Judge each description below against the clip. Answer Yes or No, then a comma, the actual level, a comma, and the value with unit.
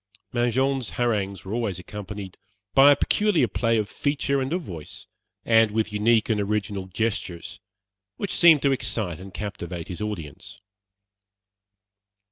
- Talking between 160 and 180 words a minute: No, slow, 135 wpm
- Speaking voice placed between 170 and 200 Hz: No, low, 105 Hz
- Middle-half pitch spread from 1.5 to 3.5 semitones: No, average, 4.4 semitones